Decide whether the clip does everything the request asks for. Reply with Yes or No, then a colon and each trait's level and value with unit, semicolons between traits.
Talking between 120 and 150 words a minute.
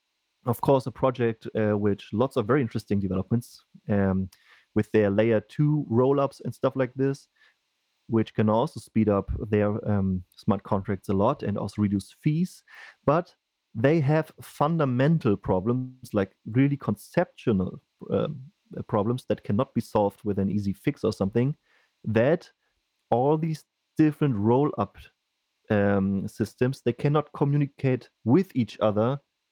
Yes: average, 140 wpm